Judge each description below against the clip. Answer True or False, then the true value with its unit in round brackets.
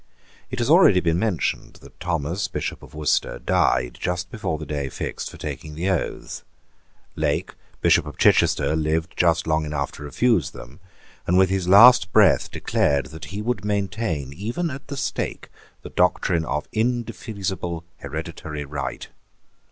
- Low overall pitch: True (90 Hz)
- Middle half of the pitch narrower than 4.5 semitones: False (5.2 semitones)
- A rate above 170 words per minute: False (155 wpm)